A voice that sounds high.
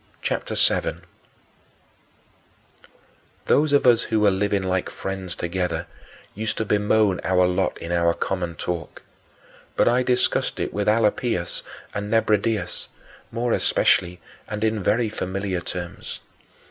No: low, 100 Hz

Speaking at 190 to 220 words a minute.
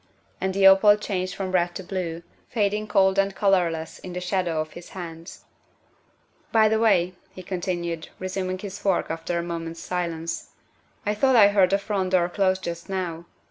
Yes: average, 200 wpm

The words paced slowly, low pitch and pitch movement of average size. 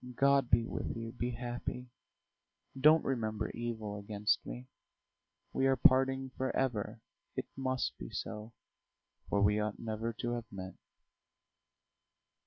Yes: slow, 125 wpm; low, 120 Hz; average, 3.5 semitones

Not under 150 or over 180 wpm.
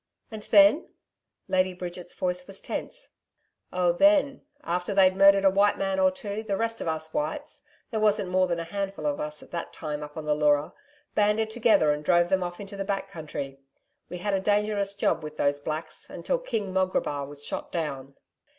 No: average, 195 wpm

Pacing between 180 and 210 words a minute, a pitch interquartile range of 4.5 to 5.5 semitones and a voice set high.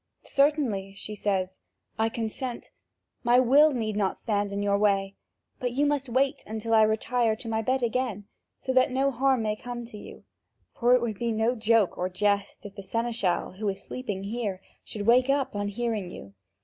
No: average, 190 wpm; average, 3.5 semitones; high, 225 Hz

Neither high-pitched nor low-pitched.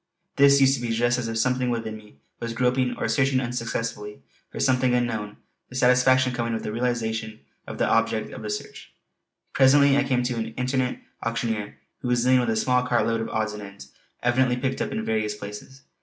No: low, 120 Hz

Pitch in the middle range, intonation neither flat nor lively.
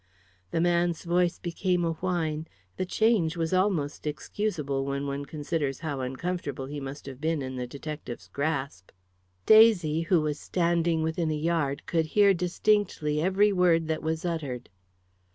Yes: medium, 160 Hz; average, 3.6 semitones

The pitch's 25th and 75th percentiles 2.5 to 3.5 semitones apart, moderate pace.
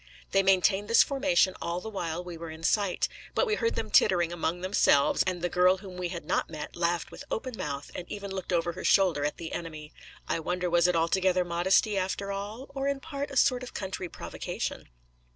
No: average, 3.0 semitones; fast, 215 wpm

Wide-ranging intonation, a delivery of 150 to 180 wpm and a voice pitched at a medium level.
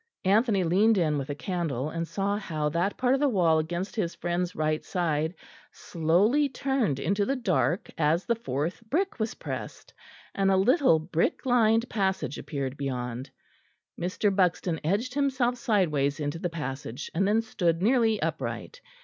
Yes: wide, 6.1 semitones; average, 160 wpm; medium, 180 Hz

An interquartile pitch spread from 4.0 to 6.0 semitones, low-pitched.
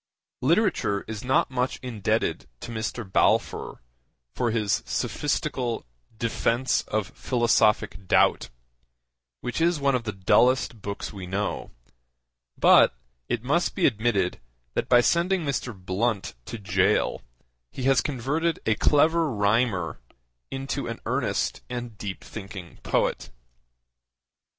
Yes: average, 4.6 semitones; low, 120 Hz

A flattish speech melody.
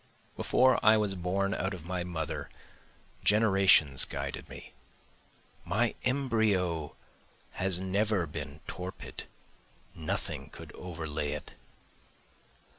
No: average, 4.2 semitones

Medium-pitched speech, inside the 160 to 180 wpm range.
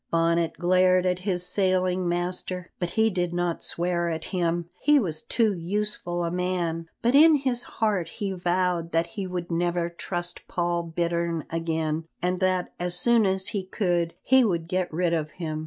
Yes: medium, 175 Hz; average, 175 wpm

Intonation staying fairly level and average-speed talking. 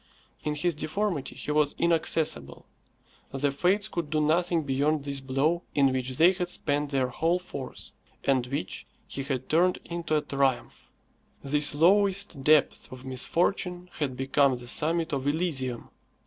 No: average, 4.1 semitones; average, 150 wpm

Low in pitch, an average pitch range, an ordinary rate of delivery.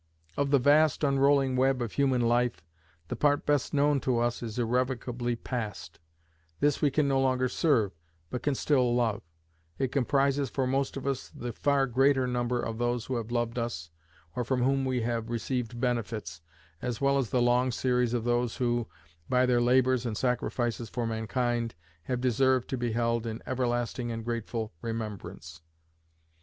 No: low, 125 Hz; narrow, 2.1 semitones; average, 175 wpm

